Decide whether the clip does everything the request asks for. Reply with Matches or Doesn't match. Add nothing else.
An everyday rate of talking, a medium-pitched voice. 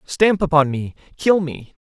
Matches